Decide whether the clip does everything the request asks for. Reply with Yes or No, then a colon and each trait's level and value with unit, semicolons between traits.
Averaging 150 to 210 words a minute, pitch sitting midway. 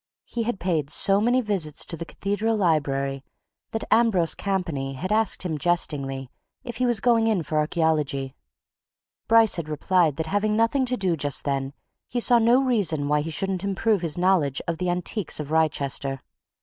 Yes: average, 175 wpm; medium, 175 Hz